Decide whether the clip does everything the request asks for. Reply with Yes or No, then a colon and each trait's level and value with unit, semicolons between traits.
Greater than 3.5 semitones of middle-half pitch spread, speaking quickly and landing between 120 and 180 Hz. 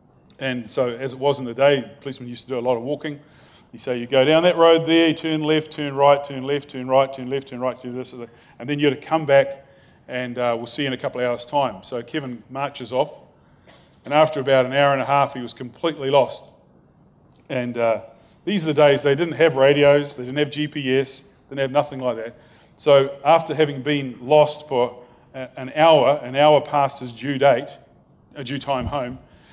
No: average, 2.7 semitones; fast, 230 wpm; medium, 140 Hz